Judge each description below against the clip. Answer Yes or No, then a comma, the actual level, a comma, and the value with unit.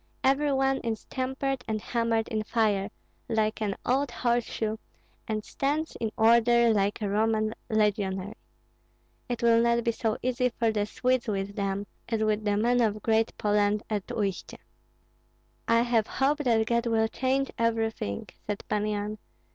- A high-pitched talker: Yes, high, 225 Hz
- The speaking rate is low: No, average, 155 wpm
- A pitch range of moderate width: No, narrow, 2.2 semitones